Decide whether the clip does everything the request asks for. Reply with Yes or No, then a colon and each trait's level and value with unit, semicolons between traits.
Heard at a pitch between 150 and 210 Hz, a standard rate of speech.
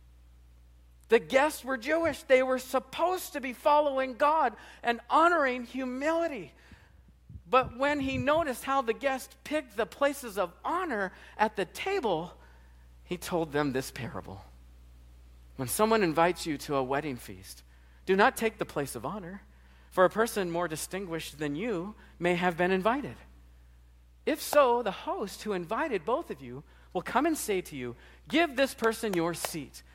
Yes: high, 190 Hz; average, 160 wpm